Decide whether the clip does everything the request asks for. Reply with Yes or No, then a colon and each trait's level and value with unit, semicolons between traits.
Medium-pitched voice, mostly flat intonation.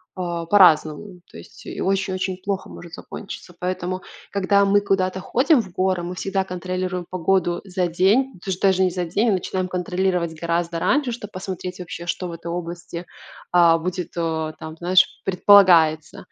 Yes: medium, 180 Hz; narrow, 1.9 semitones